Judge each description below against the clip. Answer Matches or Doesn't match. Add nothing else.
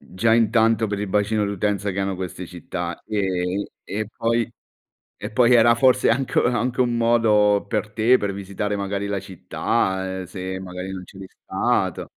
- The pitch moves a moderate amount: Matches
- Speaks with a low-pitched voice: Matches